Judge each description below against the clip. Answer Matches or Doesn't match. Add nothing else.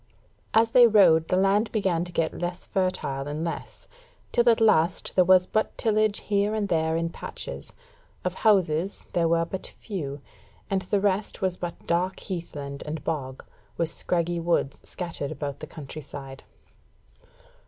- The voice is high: Doesn't match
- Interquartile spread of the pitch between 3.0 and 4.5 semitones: Matches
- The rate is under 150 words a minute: Doesn't match